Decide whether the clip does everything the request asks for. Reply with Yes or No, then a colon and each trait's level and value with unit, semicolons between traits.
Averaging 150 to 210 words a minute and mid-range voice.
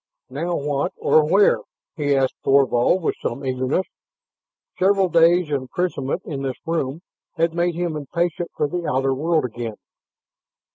No: average, 140 wpm; medium, 155 Hz